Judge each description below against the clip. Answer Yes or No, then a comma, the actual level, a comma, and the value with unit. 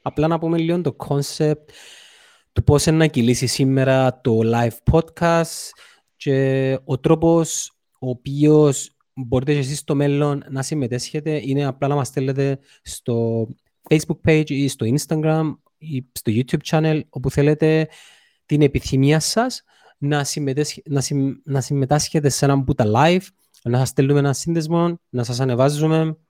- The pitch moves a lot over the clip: No, average, 2.9 semitones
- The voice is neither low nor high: Yes, medium, 145 Hz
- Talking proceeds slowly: No, average, 145 wpm